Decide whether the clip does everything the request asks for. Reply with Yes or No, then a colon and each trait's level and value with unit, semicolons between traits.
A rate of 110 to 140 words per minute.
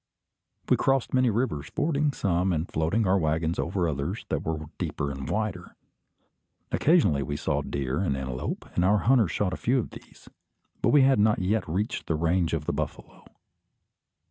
No: average, 175 wpm